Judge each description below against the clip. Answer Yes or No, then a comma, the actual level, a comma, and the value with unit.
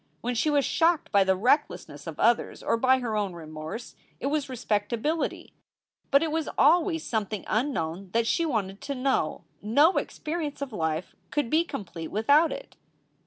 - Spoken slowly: No, average, 170 wpm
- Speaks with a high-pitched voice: Yes, high, 245 Hz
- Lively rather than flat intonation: Yes, wide, 6.8 semitones